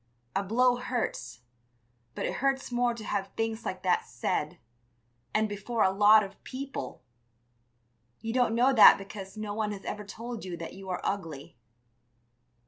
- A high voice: Yes, high, 210 Hz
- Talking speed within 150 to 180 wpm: Yes, average, 160 wpm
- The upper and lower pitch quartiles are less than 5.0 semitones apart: Yes, average, 3.5 semitones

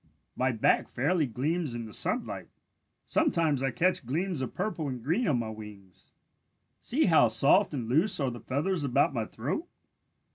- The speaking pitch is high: No, medium, 140 Hz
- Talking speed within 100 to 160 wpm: No, average, 170 wpm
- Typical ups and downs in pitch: No, wide, 6.1 semitones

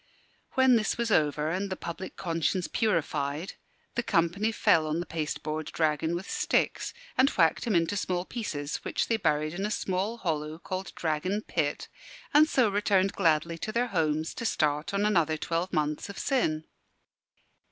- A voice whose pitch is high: No, medium, 170 Hz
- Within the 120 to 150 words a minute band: No, average, 165 wpm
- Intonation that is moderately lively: Yes, average, 4.8 semitones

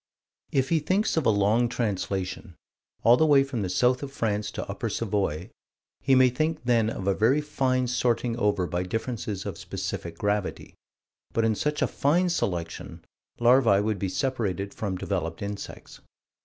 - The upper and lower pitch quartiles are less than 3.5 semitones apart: No, average, 4.6 semitones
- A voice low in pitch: Yes, low, 115 Hz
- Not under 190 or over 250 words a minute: No, average, 170 wpm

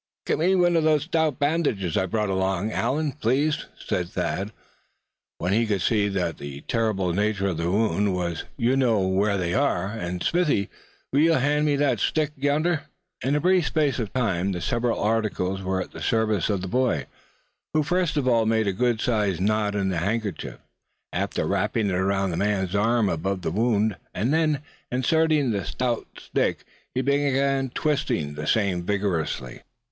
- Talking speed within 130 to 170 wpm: No, average, 180 wpm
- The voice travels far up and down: Yes, wide, 6.6 semitones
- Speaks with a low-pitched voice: Yes, low, 110 Hz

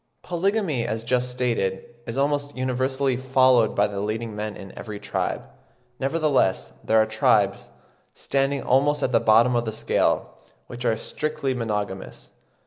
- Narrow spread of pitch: No, average, 3.8 semitones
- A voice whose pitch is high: No, low, 125 Hz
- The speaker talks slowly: No, average, 145 wpm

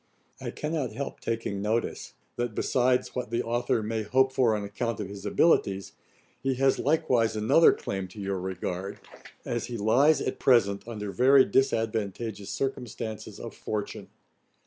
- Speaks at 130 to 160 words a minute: Yes, average, 150 wpm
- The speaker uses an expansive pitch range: No, average, 3.9 semitones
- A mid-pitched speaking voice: No, low, 115 Hz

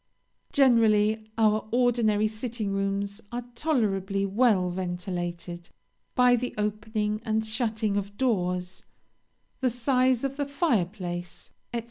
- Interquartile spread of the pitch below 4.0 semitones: Yes, average, 3.5 semitones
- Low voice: No, high, 215 Hz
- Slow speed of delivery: Yes, slow, 115 wpm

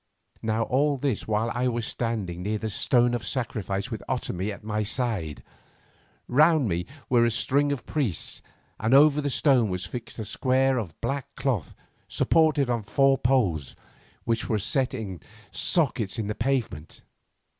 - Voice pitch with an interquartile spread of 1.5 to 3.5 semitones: No, average, 4.1 semitones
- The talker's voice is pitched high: No, low, 115 Hz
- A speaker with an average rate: Yes, average, 160 wpm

